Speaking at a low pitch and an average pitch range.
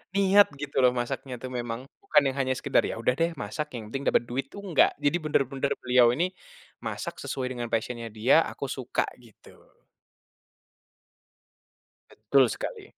Yes: low, 130 Hz; average, 3.3 semitones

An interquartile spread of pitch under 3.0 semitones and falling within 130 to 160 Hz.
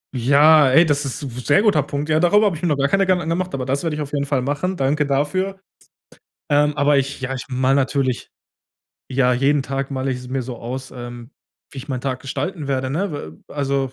Yes: narrow, 2.5 semitones; medium, 140 Hz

